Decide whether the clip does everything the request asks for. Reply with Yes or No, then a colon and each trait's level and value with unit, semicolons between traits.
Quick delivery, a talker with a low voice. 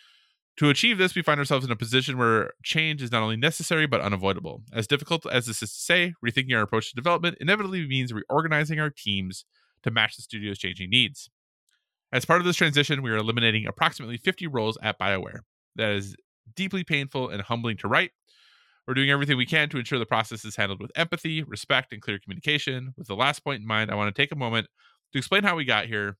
Yes: fast, 220 wpm; low, 125 Hz